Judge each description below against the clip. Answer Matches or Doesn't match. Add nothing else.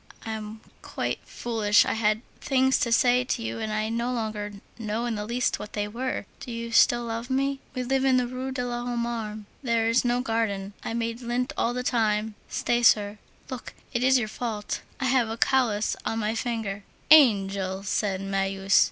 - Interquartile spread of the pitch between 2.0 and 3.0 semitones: Matches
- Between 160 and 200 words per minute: Matches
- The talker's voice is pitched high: Matches